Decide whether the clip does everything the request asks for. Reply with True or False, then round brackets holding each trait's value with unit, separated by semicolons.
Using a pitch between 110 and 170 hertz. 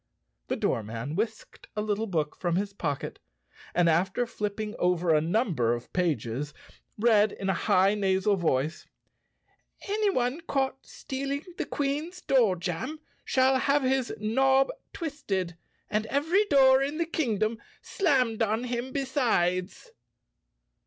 False (215 Hz)